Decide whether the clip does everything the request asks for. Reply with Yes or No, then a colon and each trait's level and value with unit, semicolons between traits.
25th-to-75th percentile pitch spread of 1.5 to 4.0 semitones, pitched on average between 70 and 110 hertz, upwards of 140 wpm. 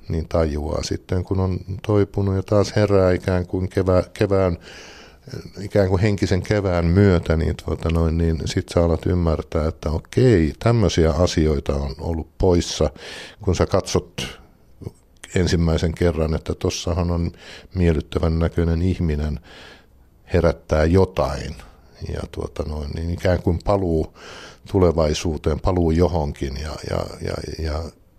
No: narrow, 2.6 semitones; very low, 85 Hz; average, 125 wpm